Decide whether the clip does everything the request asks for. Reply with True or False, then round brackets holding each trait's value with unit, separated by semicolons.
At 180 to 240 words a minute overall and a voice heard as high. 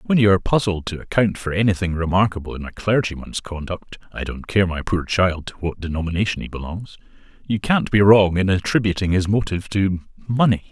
False (185 wpm; 95 Hz)